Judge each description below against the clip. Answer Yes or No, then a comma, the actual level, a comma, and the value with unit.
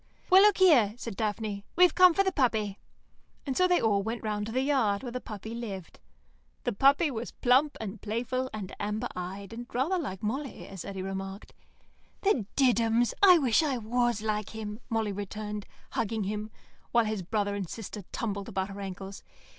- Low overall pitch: No, high, 220 Hz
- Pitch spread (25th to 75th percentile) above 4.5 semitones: No, average, 4.0 semitones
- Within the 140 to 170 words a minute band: No, average, 180 wpm